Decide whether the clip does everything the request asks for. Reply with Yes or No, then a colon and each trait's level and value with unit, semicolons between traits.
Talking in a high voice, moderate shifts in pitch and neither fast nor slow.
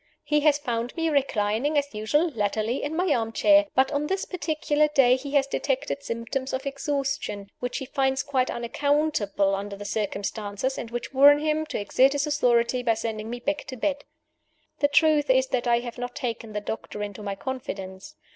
Yes: very high, 260 Hz; average, 4.5 semitones; average, 195 wpm